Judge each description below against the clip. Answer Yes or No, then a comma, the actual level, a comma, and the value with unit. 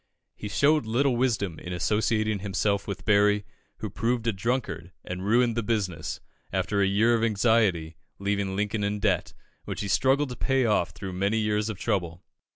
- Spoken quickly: No, average, 175 wpm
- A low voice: Yes, low, 105 Hz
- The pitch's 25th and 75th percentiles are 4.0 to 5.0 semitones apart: No, average, 3.0 semitones